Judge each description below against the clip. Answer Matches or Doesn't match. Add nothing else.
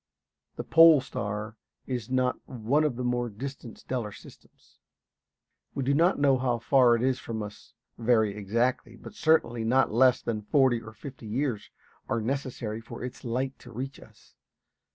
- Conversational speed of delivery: Matches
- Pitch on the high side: Doesn't match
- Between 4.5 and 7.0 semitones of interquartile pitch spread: Doesn't match